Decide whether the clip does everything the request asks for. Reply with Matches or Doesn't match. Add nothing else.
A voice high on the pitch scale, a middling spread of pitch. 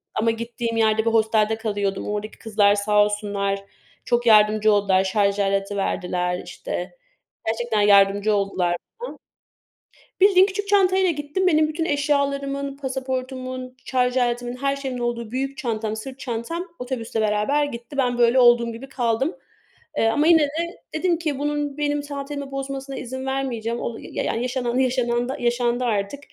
Matches